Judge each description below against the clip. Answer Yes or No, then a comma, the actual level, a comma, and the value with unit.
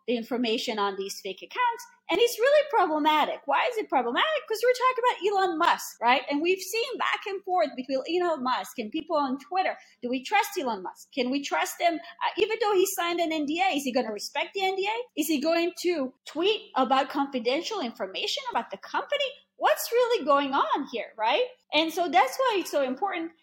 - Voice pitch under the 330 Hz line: No, very high, 340 Hz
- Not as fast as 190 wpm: No, fast, 205 wpm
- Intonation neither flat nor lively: No, wide, 7.0 semitones